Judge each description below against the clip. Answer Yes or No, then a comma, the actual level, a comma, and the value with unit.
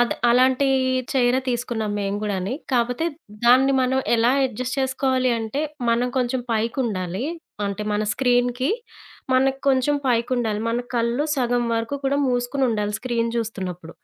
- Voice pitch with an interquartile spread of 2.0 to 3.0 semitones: Yes, narrow, 2.5 semitones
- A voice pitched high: Yes, high, 245 Hz